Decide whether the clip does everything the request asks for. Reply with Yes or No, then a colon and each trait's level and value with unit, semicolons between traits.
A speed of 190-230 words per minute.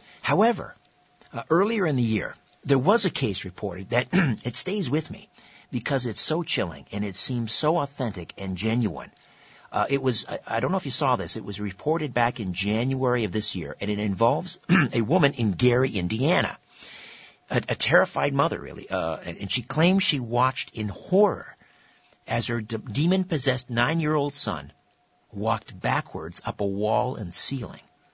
No: average, 180 wpm